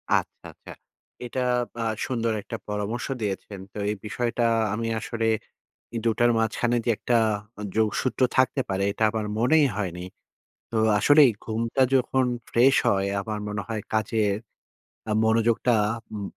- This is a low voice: Yes, low, 115 Hz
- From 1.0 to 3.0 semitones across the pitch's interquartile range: Yes, narrow, 2.4 semitones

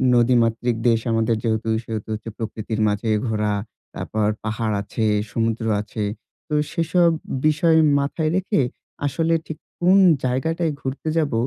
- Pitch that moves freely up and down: Yes, wide, 6.0 semitones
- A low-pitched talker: Yes, low, 115 Hz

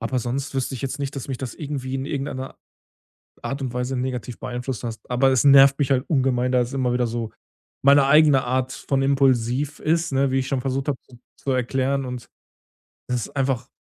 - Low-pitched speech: Yes, low, 130 Hz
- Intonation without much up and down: Yes, narrow, 1.7 semitones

